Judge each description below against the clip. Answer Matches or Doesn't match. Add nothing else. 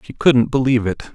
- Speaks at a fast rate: Matches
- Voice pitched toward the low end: Matches